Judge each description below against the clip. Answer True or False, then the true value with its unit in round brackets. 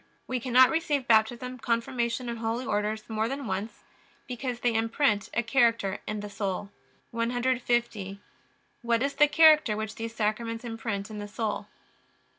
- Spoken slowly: False (155 wpm)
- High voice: True (230 Hz)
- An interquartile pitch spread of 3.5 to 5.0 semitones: False (2.5 semitones)